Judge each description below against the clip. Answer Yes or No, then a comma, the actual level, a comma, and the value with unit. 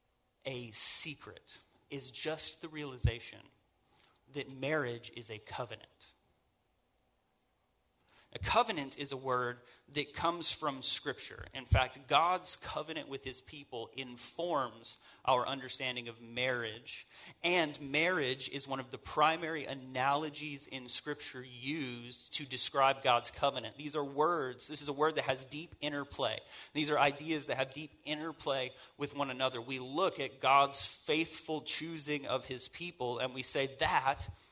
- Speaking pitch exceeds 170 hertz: No, low, 135 Hz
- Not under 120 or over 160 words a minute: Yes, average, 140 wpm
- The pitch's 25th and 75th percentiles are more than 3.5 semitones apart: No, average, 2.8 semitones